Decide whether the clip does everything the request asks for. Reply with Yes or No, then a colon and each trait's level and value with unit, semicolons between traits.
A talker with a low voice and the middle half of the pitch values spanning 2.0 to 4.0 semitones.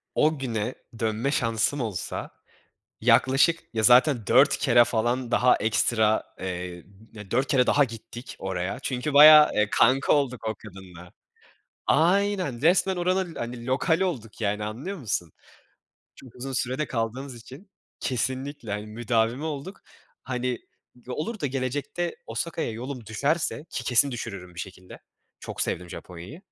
No: low, 125 Hz; average, 4.7 semitones